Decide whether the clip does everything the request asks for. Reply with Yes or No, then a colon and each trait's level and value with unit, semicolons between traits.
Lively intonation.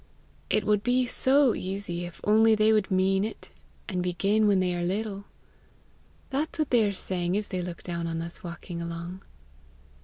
No: average, 3.6 semitones